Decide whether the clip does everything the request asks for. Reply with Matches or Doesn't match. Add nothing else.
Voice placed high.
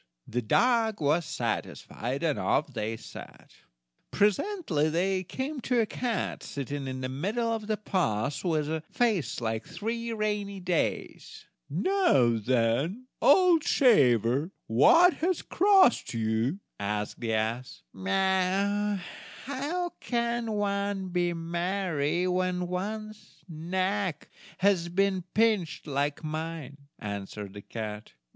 Doesn't match